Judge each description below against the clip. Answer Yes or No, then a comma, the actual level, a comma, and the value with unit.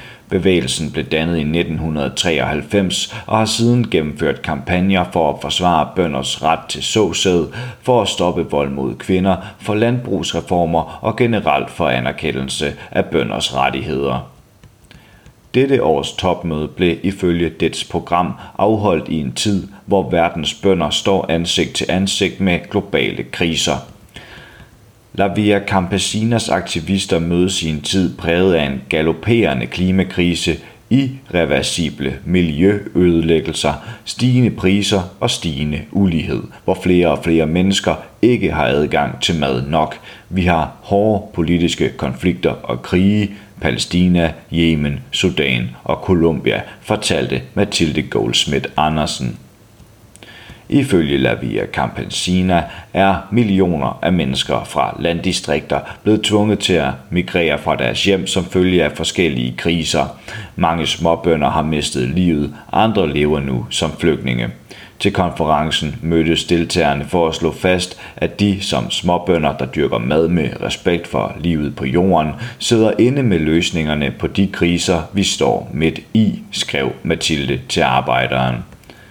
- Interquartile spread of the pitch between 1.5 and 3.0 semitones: No, average, 4.2 semitones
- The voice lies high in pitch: No, very low, 85 Hz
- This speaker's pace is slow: Yes, slow, 125 wpm